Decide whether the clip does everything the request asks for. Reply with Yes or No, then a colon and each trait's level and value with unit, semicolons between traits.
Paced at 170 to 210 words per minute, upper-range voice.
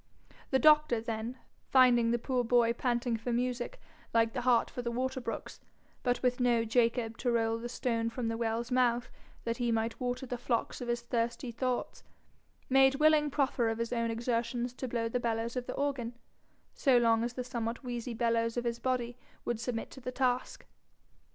Yes: average, 190 wpm; high, 240 Hz